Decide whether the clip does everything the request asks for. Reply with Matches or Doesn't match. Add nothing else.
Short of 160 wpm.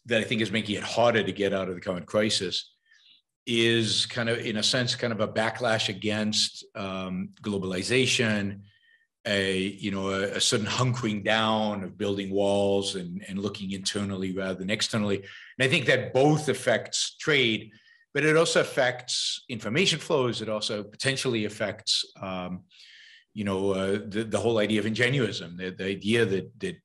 Doesn't match